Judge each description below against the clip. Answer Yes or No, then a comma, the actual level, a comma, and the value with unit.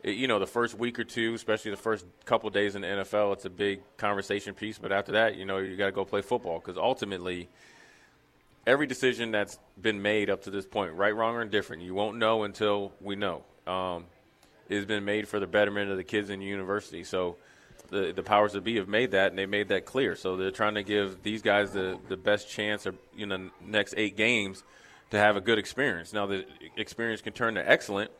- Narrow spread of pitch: Yes, narrow, 1.7 semitones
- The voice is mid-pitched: No, low, 105 Hz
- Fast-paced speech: Yes, fast, 235 wpm